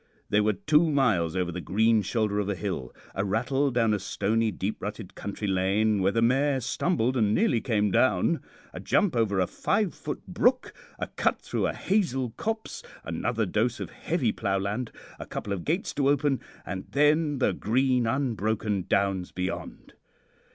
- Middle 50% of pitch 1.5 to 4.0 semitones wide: No, wide, 5.5 semitones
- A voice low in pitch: Yes, low, 110 Hz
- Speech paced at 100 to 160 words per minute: No, average, 170 wpm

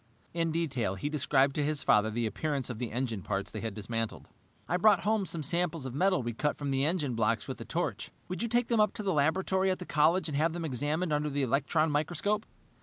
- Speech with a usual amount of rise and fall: No, wide, 5.7 semitones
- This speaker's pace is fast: Yes, fast, 240 wpm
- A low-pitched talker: No, medium, 150 Hz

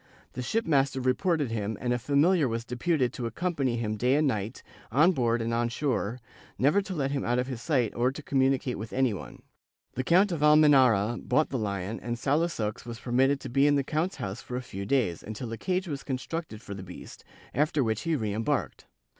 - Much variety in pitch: No, average, 4.2 semitones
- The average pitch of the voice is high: No, low, 130 Hz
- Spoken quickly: Yes, fast, 215 wpm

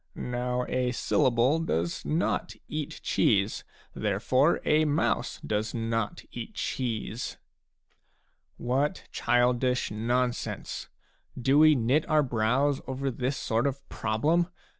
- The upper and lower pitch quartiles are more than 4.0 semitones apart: No, average, 3.7 semitones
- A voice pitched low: Yes, low, 125 Hz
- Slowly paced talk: Yes, slow, 115 wpm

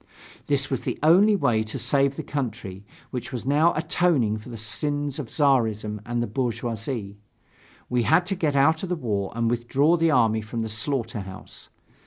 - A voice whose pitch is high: No, low, 125 Hz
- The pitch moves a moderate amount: Yes, average, 4.8 semitones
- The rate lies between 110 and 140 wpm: No, average, 185 wpm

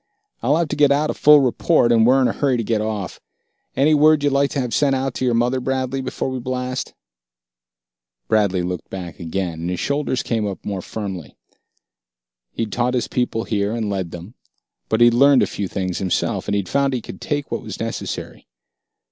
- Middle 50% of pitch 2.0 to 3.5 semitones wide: No, average, 5.1 semitones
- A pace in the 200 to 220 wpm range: Yes, fast, 205 wpm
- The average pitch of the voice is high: No, low, 120 Hz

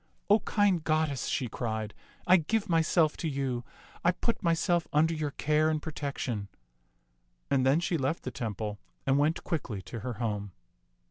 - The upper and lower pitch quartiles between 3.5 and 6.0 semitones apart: Yes, average, 5.3 semitones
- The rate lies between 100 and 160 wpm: No, average, 175 wpm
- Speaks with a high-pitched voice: No, medium, 150 Hz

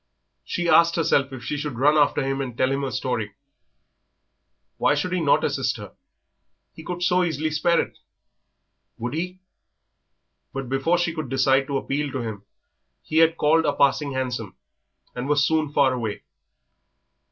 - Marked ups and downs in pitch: No, average, 3.4 semitones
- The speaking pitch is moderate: Yes, medium, 145 Hz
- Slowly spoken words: No, average, 165 wpm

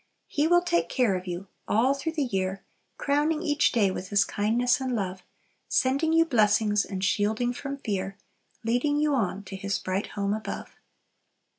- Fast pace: No, average, 170 wpm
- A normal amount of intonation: No, wide, 6.1 semitones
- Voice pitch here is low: No, high, 220 Hz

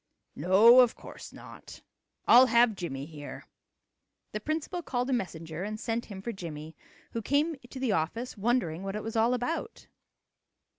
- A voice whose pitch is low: No, high, 225 Hz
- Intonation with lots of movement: Yes, wide, 5.8 semitones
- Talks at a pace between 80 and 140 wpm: No, average, 160 wpm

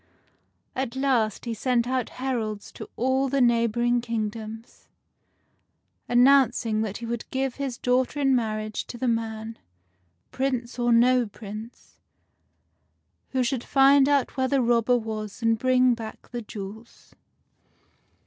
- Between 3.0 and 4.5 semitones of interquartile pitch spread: No, narrow, 2.6 semitones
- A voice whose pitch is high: Yes, high, 240 Hz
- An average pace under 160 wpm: Yes, average, 140 wpm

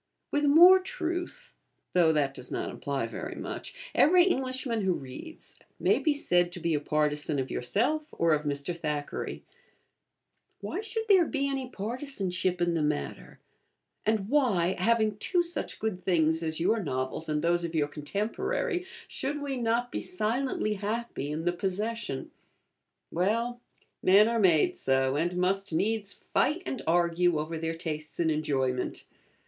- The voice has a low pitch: No, medium, 185 Hz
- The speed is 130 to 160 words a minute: Yes, average, 155 wpm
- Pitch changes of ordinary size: No, wide, 8.4 semitones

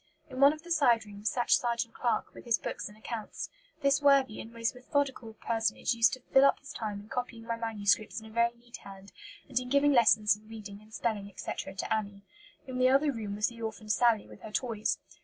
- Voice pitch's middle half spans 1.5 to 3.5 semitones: Yes, average, 3.0 semitones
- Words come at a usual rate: No, fast, 225 wpm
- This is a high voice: Yes, high, 230 Hz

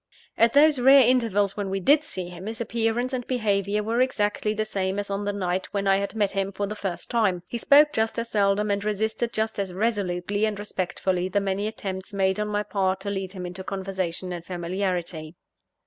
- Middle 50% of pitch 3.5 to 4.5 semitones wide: No, average, 2.7 semitones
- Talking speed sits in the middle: No, fast, 210 wpm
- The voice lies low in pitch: No, high, 200 Hz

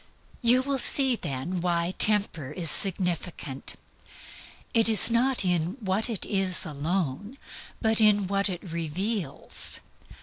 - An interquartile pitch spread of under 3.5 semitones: No, average, 4.7 semitones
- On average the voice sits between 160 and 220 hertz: Yes, high, 190 Hz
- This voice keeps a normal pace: No, slow, 125 wpm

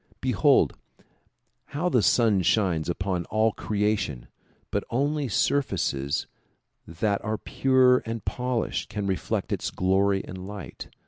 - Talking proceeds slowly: Yes, slow, 120 wpm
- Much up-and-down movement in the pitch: No, average, 4.8 semitones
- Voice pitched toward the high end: No, low, 105 Hz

